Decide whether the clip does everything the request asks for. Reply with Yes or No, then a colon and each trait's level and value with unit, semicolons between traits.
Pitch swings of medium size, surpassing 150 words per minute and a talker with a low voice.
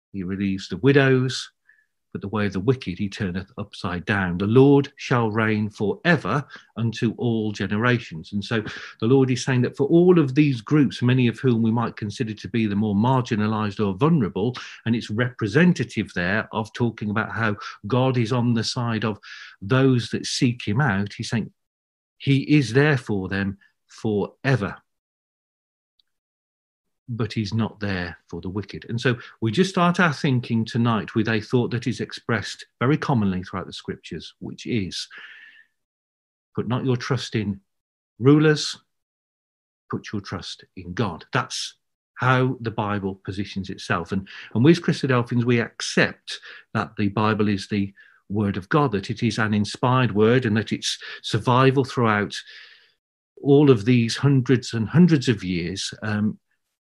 Yes: average, 4.2 semitones; average, 160 wpm; low, 115 Hz